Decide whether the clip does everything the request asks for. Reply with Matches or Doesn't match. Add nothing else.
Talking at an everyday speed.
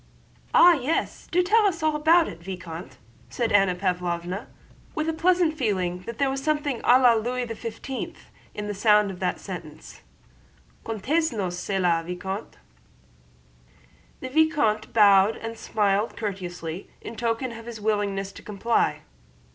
Matches